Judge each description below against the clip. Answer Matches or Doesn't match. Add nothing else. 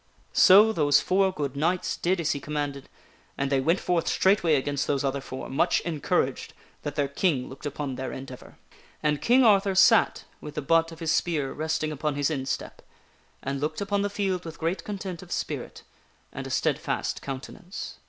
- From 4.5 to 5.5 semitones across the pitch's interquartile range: Matches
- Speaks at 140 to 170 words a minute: Doesn't match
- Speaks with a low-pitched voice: Doesn't match